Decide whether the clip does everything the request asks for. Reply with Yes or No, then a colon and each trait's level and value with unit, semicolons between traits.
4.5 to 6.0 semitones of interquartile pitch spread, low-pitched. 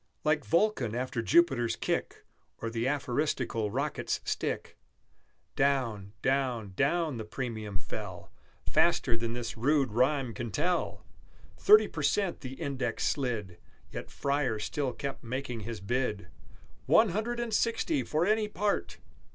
Yes: average, 5.1 semitones; low, 130 Hz